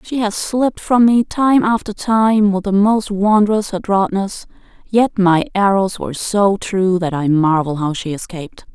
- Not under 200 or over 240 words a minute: No, average, 170 wpm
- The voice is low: No, high, 200 Hz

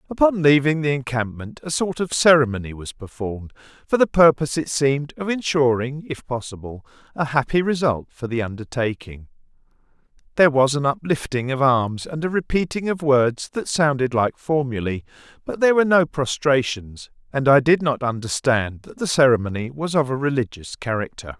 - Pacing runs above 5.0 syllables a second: Yes, 5.3 syllables/s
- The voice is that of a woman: No, male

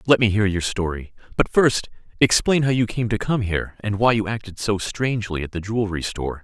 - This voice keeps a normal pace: No, fast, 225 wpm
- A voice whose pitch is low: Yes, low, 105 Hz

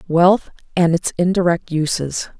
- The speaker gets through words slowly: Yes, slow, 125 wpm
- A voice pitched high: No, medium, 170 Hz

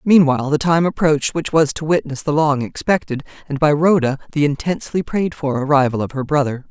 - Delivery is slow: No, average, 195 wpm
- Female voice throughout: Yes, female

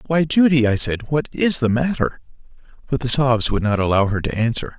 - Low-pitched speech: Yes, low, 130 Hz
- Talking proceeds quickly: Yes, fast, 215 wpm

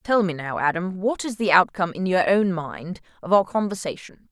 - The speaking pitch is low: No, medium, 185 Hz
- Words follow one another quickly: Yes, fast, 210 wpm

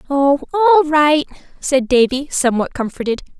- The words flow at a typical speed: No, slow, 125 wpm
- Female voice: Yes, female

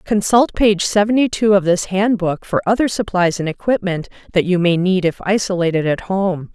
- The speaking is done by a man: No, female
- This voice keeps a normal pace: Yes, average, 185 wpm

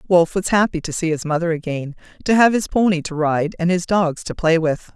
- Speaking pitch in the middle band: Yes, medium, 170 Hz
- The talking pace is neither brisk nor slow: No, fast, 240 wpm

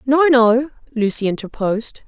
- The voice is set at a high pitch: Yes, high, 245 Hz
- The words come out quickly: No, slow, 115 wpm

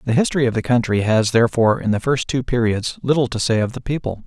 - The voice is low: Yes, low, 120 Hz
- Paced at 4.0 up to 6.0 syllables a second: No, 6.6 syllables/s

